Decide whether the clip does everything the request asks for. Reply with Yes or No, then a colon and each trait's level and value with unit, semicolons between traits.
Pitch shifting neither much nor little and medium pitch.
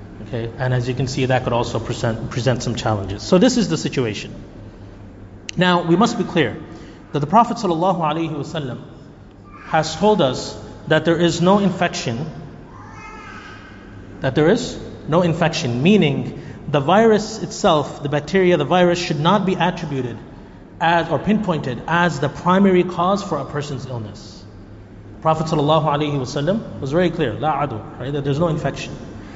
No: wide, 6.8 semitones; medium, 145 Hz